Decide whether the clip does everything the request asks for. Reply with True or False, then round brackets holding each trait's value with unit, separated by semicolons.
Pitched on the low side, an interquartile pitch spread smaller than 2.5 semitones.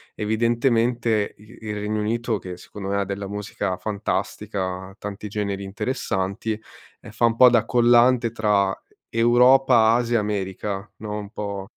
False (105 Hz; 2.8 semitones)